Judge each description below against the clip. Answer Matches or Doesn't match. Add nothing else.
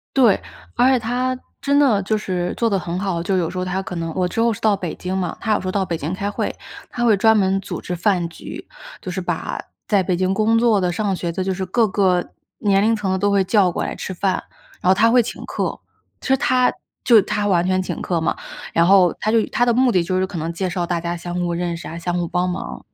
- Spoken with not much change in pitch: Doesn't match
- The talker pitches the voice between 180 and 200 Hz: Matches